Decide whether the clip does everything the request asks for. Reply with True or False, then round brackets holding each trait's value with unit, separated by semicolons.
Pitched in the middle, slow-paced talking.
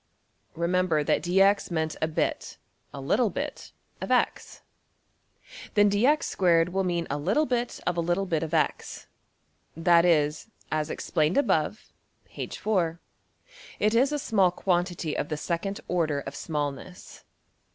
True (175 Hz; 130 wpm)